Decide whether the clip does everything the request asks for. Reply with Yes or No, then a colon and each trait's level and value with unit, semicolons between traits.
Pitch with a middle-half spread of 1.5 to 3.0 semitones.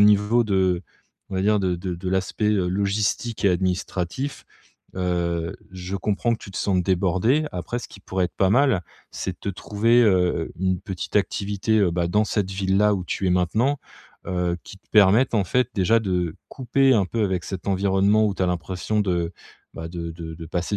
Yes: average, 2.7 semitones